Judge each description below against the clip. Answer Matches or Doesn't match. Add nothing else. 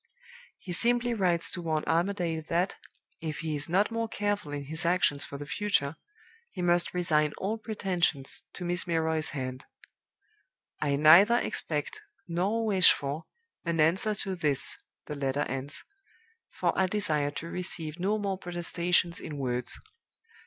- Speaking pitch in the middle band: Matches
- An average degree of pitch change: Matches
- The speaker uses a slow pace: Doesn't match